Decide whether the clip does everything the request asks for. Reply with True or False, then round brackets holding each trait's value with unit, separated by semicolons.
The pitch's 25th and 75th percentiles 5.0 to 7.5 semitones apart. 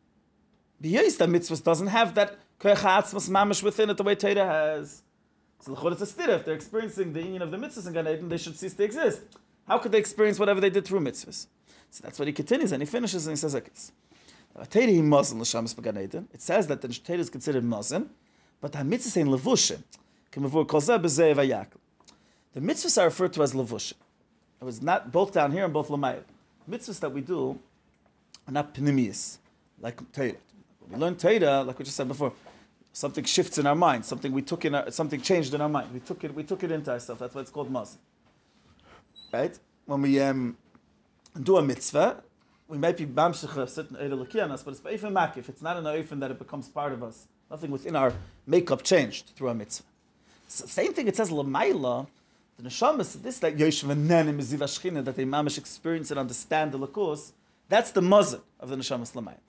True (5.5 semitones)